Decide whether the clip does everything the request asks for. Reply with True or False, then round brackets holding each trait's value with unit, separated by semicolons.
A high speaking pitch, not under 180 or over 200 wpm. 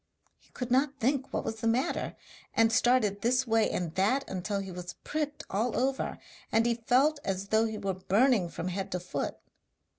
True (225 Hz; 190 wpm)